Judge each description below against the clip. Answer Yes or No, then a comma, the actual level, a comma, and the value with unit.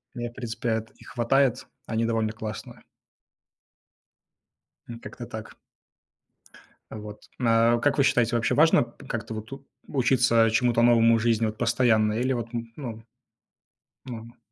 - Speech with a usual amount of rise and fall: No, narrow, 1.4 semitones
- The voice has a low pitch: Yes, low, 115 Hz